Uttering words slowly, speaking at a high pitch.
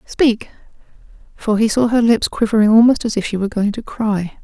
No: fast, 205 wpm; high, 220 Hz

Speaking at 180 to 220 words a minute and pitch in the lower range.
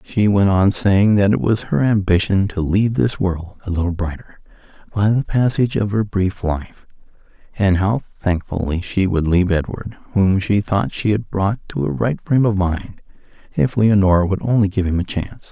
Yes: average, 195 wpm; low, 100 Hz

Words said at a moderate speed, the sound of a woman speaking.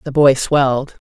Yes: average, 170 wpm; female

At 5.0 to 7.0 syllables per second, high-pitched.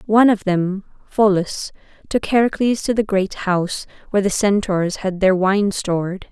No: 4.7 syllables/s; high, 195 Hz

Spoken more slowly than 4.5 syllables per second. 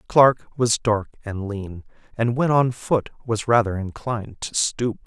Yes: 3.9 syllables/s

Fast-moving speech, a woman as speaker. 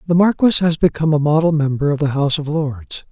No: fast, 230 wpm; male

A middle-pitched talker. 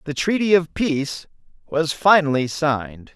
Yes: medium, 155 Hz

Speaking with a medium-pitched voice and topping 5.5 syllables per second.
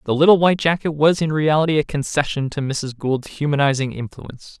Yes: medium, 145 Hz; 5.9 syllables/s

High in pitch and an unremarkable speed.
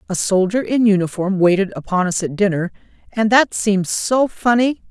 Yes: high, 205 Hz; average, 170 wpm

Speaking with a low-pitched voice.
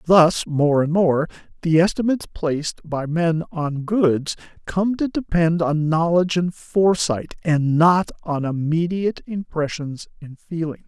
No: medium, 165 Hz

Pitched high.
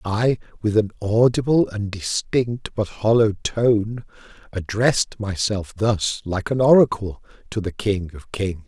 No: low, 105 Hz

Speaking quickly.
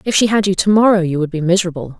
Yes: fast, 300 wpm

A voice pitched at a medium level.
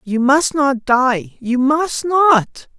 No: very high, 265 Hz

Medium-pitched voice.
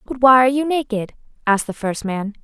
No: high, 235 Hz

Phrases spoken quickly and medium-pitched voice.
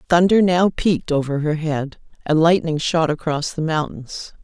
No: average, 160 wpm; medium, 160 Hz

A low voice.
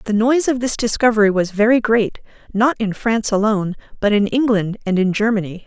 No: high, 215 Hz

